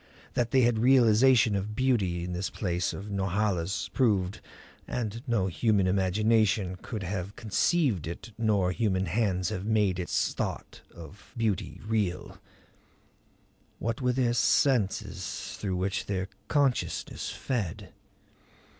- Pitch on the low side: Yes, low, 105 Hz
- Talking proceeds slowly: Yes, slow, 120 wpm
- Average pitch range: Yes, average, 3.7 semitones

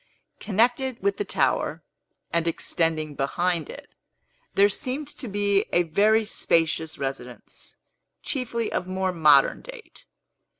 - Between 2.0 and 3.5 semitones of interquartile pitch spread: No, wide, 5.5 semitones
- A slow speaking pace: Yes, slow, 120 wpm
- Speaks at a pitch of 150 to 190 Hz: Yes, medium, 185 Hz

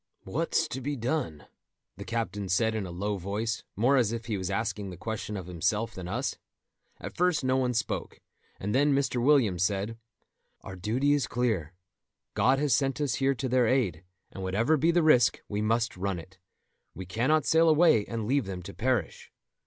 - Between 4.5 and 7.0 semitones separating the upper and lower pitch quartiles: Yes, average, 5.2 semitones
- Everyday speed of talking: Yes, average, 190 wpm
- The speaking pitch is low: Yes, low, 115 Hz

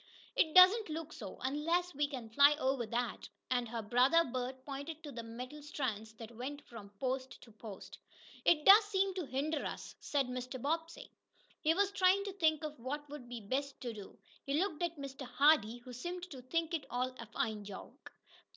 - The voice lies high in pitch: Yes, very high, 275 Hz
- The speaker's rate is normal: Yes, average, 195 wpm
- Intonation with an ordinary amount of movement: Yes, average, 4.8 semitones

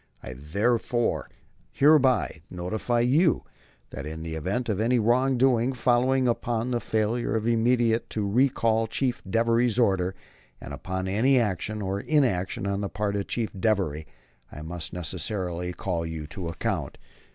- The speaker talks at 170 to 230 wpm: No, average, 145 wpm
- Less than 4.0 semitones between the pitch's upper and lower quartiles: No, average, 4.7 semitones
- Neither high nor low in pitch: No, low, 110 Hz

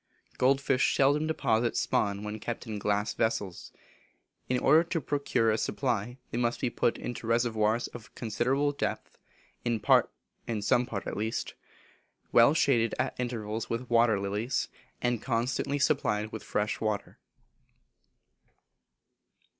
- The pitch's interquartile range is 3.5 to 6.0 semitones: No, average, 2.8 semitones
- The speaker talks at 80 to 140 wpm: Yes, slow, 135 wpm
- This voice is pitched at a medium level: No, low, 115 Hz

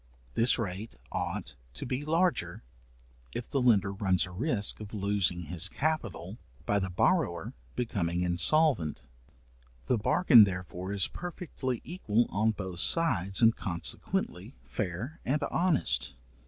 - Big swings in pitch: Yes, wide, 6.1 semitones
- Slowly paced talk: Yes, slow, 125 wpm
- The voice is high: No, low, 105 Hz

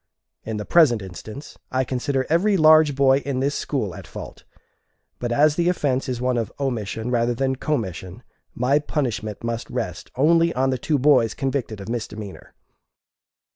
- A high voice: No, low, 130 Hz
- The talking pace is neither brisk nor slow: Yes, average, 165 wpm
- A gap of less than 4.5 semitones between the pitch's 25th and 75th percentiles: Yes, average, 3.9 semitones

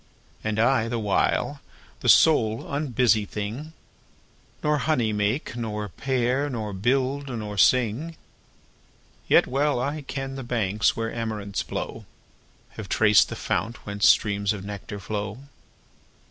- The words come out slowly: Yes, slow, 130 wpm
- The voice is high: No, low, 115 Hz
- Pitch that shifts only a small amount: No, average, 4.4 semitones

